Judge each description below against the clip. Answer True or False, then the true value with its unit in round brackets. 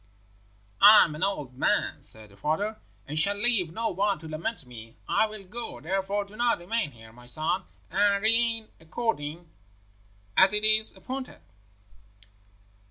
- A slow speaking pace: False (155 wpm)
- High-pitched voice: True (195 Hz)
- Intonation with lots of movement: True (5.8 semitones)